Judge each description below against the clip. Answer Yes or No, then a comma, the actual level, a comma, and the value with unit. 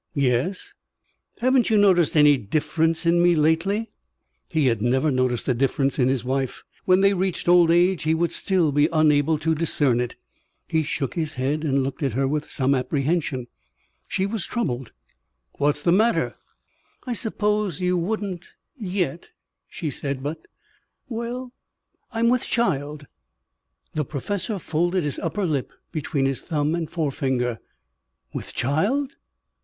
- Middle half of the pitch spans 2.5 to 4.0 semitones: No, average, 5.2 semitones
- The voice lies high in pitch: No, medium, 160 Hz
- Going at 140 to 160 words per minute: Yes, average, 150 wpm